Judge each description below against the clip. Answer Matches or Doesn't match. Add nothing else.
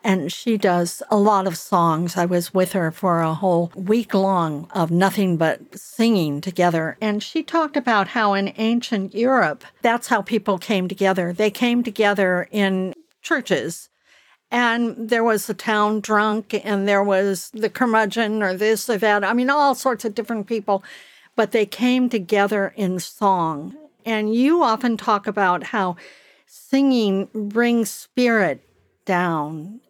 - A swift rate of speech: Doesn't match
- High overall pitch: Matches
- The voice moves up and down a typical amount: Matches